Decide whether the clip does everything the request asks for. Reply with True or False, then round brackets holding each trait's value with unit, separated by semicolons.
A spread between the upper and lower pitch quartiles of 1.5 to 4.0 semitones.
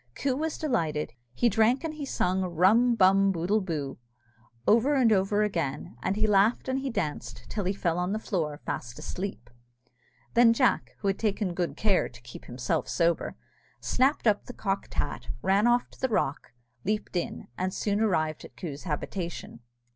False (5.1 semitones)